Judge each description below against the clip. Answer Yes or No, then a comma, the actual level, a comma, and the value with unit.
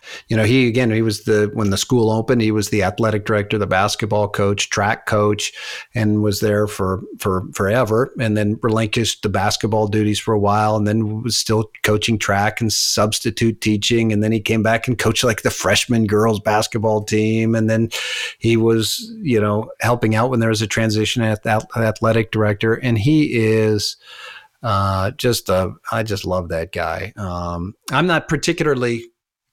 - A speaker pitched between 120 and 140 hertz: No, low, 110 Hz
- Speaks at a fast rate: No, average, 180 wpm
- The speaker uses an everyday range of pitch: No, narrow, 1.5 semitones